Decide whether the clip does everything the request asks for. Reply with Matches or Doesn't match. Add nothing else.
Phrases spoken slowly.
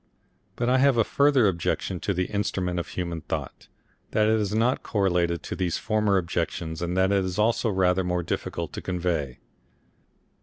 Doesn't match